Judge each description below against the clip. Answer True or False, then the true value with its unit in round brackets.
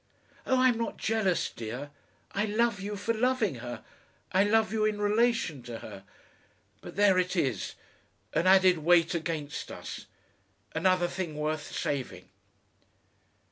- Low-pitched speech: False (185 Hz)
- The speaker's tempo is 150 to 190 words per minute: False (140 wpm)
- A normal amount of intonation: False (6.0 semitones)